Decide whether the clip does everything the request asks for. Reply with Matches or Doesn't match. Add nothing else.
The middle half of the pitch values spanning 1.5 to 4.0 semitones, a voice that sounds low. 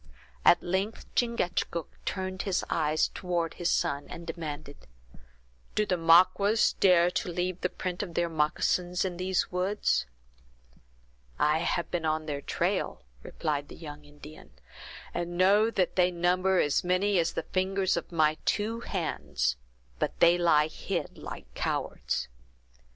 Doesn't match